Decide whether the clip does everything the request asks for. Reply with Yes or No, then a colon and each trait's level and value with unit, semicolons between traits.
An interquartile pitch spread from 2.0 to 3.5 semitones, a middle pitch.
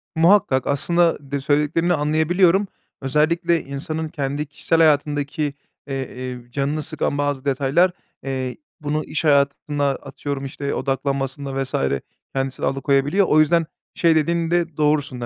Yes: average, 2.8 semitones; medium, 145 Hz